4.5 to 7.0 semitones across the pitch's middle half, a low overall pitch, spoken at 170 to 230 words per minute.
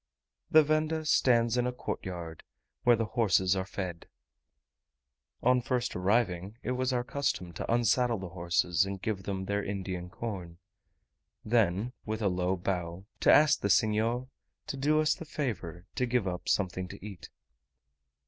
No: average, 5.1 semitones; low, 105 Hz; average, 160 wpm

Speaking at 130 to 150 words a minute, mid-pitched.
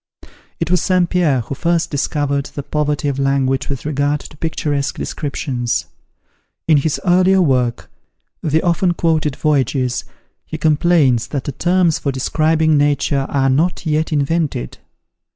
Yes: average, 140 wpm; medium, 150 Hz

